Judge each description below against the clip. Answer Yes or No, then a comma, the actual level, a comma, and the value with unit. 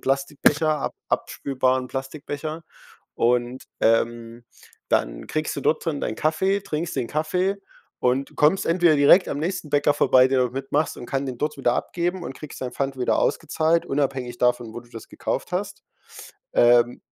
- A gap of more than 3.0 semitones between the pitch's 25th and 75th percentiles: Yes, average, 4.0 semitones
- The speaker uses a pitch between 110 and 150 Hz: Yes, medium, 140 Hz